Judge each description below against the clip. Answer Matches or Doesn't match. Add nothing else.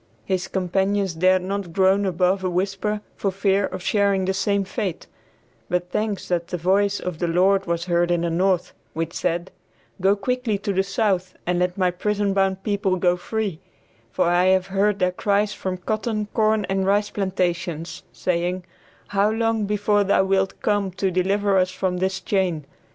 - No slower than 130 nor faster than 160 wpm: Doesn't match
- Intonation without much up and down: Matches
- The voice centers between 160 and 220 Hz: Matches